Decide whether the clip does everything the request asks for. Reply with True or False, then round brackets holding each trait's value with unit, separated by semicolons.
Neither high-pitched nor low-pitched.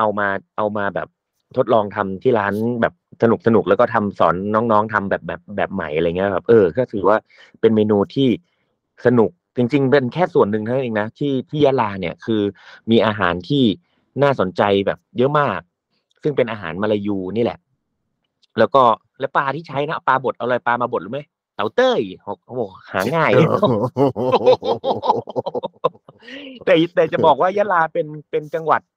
False (115 Hz)